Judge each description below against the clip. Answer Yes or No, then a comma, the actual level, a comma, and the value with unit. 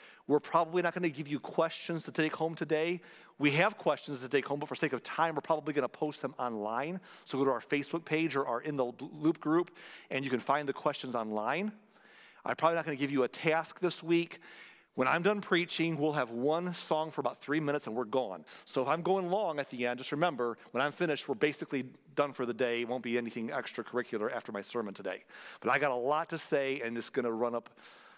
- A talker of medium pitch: Yes, medium, 150 Hz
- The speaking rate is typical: No, fast, 245 wpm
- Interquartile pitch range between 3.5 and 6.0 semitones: Yes, average, 4.5 semitones